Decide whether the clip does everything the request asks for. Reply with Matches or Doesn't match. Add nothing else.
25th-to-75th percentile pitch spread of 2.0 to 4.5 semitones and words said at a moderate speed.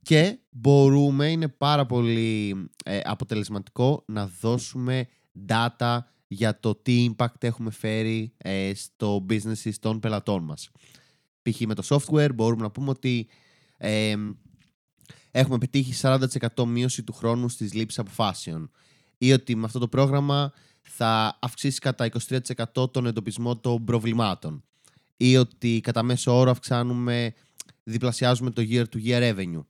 Matches